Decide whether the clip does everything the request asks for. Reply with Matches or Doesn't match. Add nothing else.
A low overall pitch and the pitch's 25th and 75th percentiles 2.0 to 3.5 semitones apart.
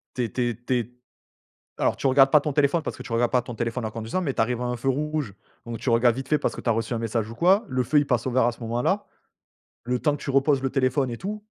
Matches